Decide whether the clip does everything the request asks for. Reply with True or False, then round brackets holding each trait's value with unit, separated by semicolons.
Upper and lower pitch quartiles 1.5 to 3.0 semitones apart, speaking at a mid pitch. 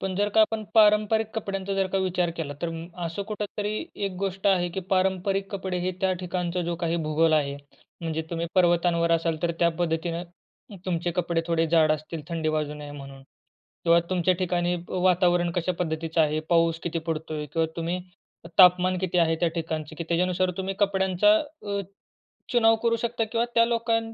True (2.7 semitones; 175 Hz)